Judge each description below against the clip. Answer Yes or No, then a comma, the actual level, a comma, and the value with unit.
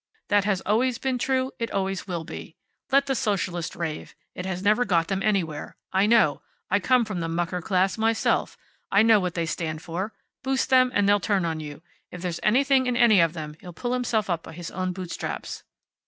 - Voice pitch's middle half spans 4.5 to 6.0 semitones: Yes, average, 4.9 semitones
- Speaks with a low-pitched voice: No, high, 195 Hz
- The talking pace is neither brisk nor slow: No, fast, 210 wpm